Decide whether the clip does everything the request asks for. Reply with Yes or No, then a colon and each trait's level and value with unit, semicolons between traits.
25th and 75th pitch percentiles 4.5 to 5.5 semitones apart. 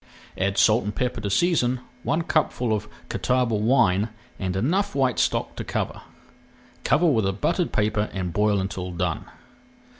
Yes: average, 4.8 semitones